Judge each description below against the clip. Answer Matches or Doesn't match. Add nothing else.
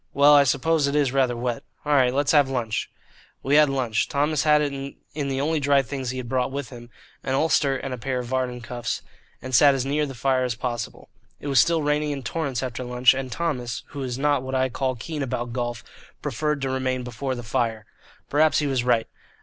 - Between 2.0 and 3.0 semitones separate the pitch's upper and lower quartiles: Matches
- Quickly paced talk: Matches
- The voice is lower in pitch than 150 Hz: Matches